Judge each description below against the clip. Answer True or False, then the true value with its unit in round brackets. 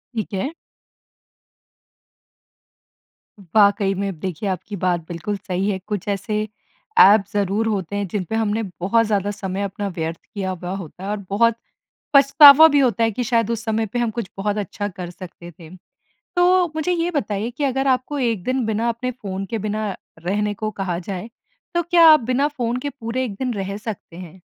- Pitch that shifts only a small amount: False (3.8 semitones)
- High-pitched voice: True (210 Hz)